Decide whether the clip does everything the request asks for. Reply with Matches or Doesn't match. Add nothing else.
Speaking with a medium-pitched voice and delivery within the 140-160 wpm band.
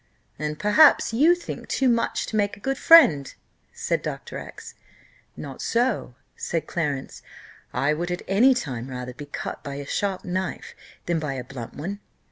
Doesn't match